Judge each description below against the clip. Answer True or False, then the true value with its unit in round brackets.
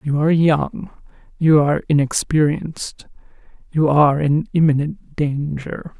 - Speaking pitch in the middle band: True (150 Hz)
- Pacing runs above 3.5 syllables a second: True (4.5 syllables/s)